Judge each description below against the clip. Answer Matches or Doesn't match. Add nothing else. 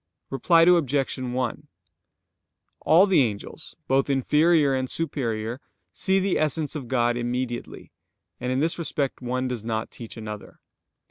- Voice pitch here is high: Doesn't match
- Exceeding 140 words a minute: Doesn't match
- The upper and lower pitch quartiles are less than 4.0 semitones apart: Doesn't match